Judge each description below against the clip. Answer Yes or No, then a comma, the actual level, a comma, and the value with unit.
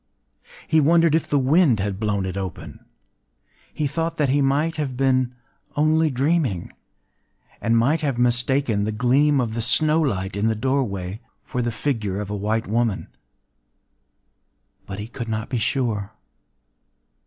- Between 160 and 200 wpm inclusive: No, average, 150 wpm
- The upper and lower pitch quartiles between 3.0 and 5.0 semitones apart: No, wide, 5.5 semitones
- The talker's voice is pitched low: Yes, low, 125 Hz